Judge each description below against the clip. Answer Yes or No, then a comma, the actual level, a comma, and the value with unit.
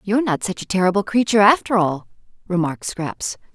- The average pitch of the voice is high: Yes, high, 195 Hz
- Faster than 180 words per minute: No, average, 170 wpm